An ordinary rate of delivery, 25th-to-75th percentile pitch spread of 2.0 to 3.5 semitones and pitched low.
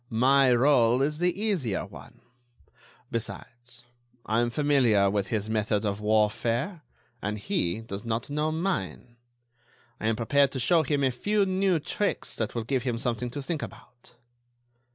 No: average, 155 wpm; average, 4.8 semitones; low, 120 Hz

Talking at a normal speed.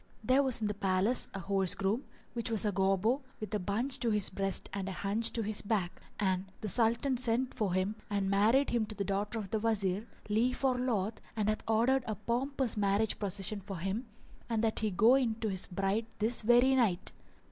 No: fast, 215 wpm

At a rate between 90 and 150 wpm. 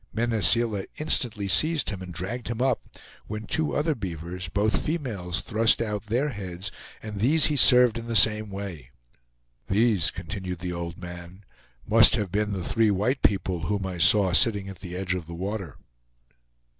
No: average, 175 wpm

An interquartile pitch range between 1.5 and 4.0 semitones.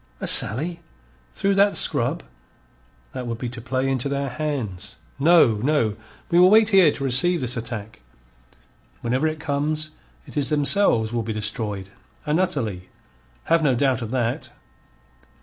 No: average, 5.2 semitones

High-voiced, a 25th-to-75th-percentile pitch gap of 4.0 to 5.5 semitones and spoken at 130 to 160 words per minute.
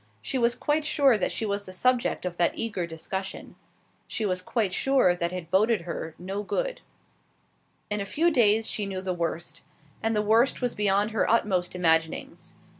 No: high, 205 Hz; average, 4.3 semitones; average, 185 wpm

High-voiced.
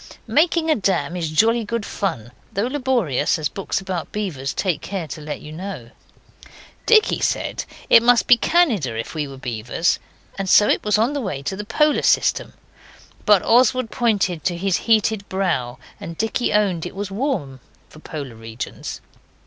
Yes: high, 195 Hz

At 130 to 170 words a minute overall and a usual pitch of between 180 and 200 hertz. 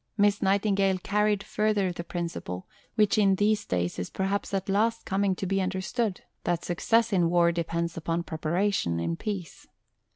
Yes: average, 160 wpm; high, 190 Hz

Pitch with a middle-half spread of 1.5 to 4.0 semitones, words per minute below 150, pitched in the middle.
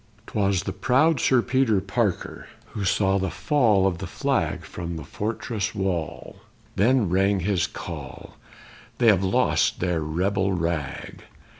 No: average, 3.7 semitones; average, 140 wpm; very low, 95 Hz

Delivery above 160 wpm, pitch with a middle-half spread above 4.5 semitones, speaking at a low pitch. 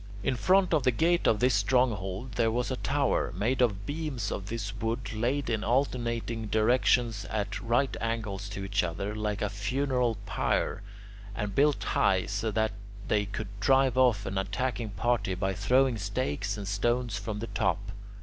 No: average, 170 wpm; average, 3.8 semitones; low, 110 Hz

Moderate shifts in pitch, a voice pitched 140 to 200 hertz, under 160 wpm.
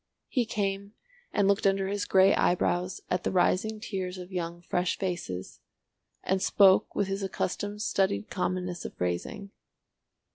No: narrow, 1.9 semitones; high, 190 Hz; average, 145 wpm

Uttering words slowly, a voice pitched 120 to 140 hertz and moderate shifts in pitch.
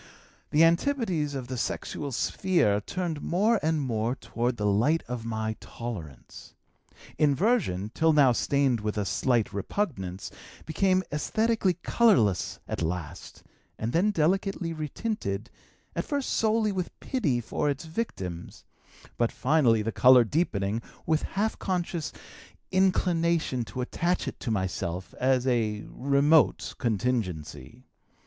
No: slow, 125 wpm; low, 135 Hz; wide, 8.0 semitones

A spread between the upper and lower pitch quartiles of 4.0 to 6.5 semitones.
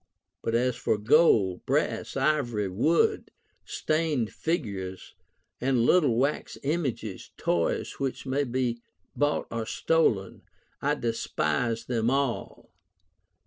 Yes: average, 4.6 semitones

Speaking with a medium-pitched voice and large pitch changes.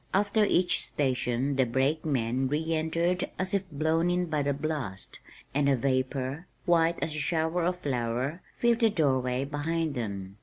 No: medium, 150 Hz; average, 4.4 semitones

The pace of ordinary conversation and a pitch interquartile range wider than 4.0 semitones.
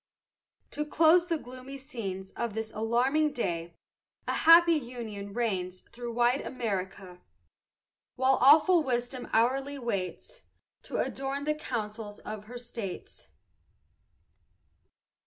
No: slow, 110 wpm; average, 4.8 semitones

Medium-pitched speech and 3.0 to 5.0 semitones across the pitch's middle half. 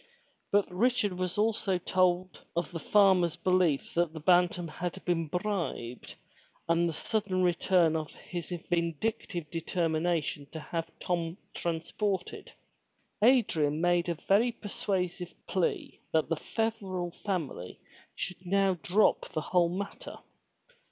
No: medium, 175 Hz; narrow, 2.5 semitones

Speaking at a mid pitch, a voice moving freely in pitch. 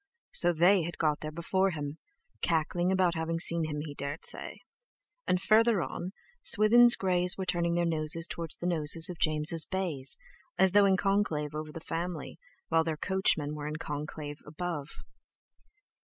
No: medium, 165 Hz; average, 3.3 semitones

